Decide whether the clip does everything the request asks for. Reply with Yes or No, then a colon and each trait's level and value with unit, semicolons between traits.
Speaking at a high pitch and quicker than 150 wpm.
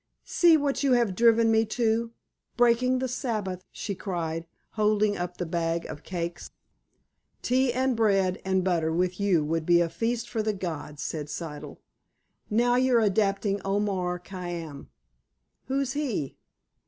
No: high, 200 Hz; average, 140 wpm